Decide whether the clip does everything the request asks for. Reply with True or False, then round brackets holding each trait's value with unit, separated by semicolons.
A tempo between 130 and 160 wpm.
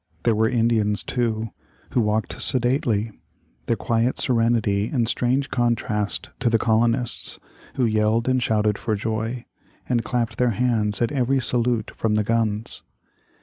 True (145 wpm)